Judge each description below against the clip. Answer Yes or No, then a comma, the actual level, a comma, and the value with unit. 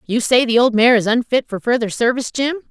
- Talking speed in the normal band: No, fast, 245 wpm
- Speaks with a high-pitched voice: Yes, high, 240 Hz